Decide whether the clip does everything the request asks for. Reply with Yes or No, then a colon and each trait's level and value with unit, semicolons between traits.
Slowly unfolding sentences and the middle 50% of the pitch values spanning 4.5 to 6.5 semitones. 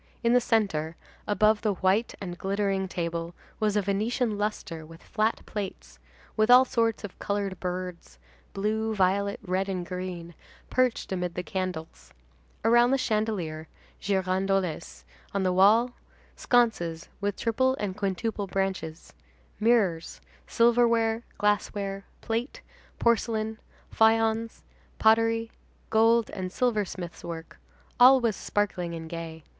No: slow, 120 wpm; average, 3.6 semitones